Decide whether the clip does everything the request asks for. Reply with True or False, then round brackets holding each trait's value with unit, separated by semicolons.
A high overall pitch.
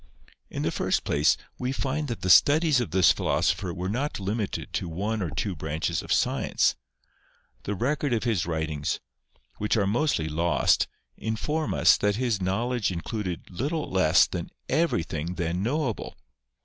False (105 Hz)